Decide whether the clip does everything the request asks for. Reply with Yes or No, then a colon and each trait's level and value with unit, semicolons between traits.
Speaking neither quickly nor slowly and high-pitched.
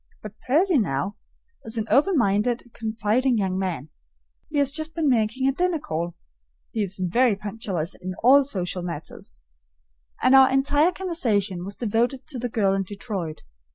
Yes: average, 160 wpm; high, 225 Hz